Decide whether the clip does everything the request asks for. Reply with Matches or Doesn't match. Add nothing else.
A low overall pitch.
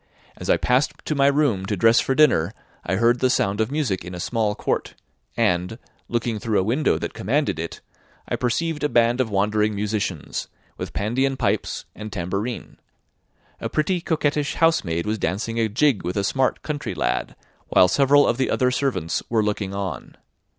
Matches